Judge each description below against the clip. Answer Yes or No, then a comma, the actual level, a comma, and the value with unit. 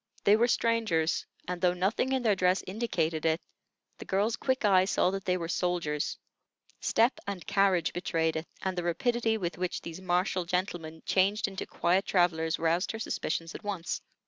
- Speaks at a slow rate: No, average, 175 wpm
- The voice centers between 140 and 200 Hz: Yes, medium, 185 Hz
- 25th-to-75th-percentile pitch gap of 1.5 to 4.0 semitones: Yes, average, 3.3 semitones